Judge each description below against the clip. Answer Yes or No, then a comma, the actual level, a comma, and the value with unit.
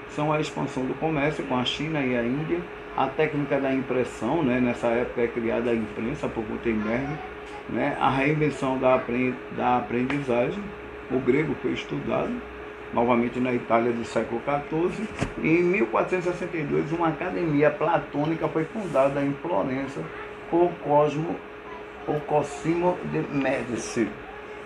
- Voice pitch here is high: No, medium, 140 Hz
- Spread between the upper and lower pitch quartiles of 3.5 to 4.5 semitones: Yes, average, 4.0 semitones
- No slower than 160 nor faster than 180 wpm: No, average, 135 wpm